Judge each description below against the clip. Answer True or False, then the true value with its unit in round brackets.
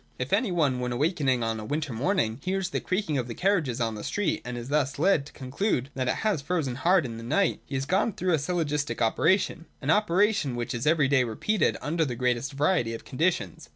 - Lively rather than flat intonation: True (6.5 semitones)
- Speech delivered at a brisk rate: True (230 wpm)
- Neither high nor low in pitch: True (145 Hz)